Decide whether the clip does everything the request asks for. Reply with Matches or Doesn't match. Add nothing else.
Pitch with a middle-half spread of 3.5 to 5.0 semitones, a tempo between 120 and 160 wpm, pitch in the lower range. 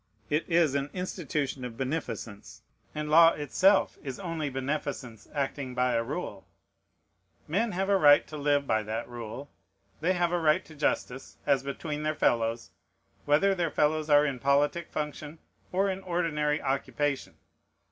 Doesn't match